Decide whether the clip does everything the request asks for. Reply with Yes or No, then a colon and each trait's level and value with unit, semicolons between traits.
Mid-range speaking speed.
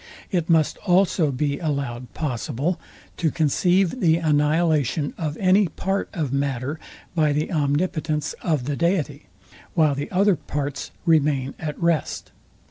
No: slow, 130 wpm